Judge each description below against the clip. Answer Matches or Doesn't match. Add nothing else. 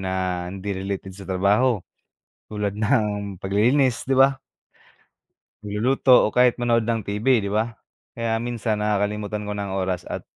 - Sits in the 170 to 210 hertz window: Doesn't match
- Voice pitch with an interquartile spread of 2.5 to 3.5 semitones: Matches